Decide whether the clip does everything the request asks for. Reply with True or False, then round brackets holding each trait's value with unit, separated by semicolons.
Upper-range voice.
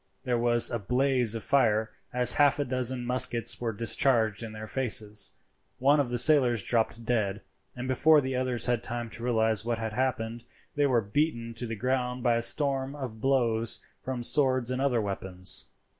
False (120 Hz)